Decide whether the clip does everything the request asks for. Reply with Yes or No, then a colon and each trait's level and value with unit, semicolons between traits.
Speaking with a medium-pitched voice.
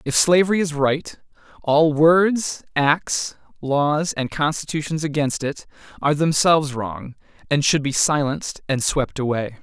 Yes: medium, 150 Hz